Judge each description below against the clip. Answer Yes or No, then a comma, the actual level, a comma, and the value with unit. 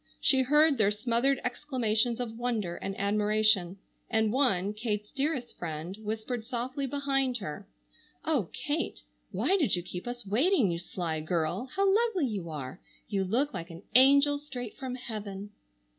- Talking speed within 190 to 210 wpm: No, average, 155 wpm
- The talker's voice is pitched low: No, high, 225 Hz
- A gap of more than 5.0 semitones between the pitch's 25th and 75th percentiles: Yes, wide, 5.4 semitones